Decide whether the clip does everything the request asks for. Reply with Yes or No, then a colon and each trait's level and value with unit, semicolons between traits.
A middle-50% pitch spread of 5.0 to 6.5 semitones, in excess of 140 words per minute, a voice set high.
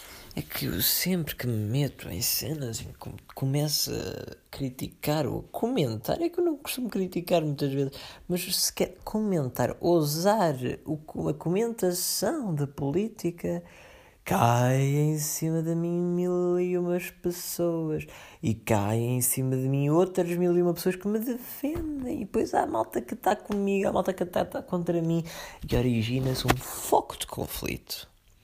No: wide, 5.6 semitones; average, 160 wpm; medium, 165 Hz